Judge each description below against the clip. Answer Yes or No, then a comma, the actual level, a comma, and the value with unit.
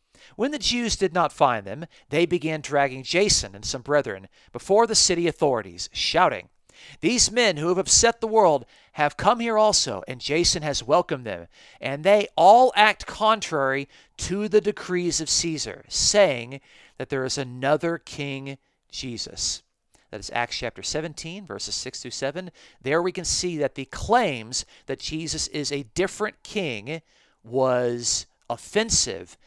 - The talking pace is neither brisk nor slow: Yes, average, 155 wpm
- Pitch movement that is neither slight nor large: No, wide, 6.2 semitones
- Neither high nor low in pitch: Yes, medium, 155 Hz